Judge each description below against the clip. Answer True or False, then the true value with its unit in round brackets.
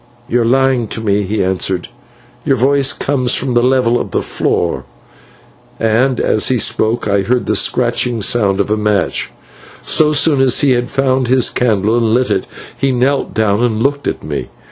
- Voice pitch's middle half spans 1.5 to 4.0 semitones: True (3.3 semitones)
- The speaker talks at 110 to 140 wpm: False (190 wpm)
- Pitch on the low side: True (120 Hz)